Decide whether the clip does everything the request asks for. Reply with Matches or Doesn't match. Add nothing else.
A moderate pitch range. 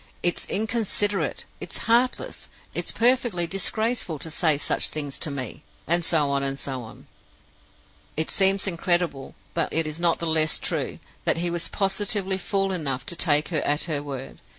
Matches